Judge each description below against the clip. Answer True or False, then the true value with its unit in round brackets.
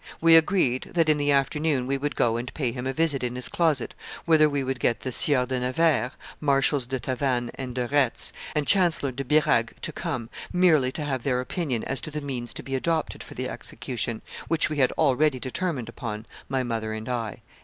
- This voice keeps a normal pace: False (210 wpm)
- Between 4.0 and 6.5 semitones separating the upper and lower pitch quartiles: False (3.5 semitones)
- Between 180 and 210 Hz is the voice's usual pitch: False (135 Hz)